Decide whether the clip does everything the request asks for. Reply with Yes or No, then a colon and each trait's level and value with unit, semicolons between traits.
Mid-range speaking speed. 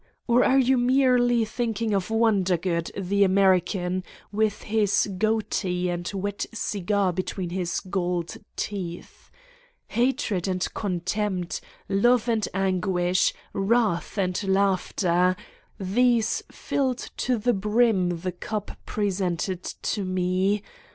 No: slow, 115 wpm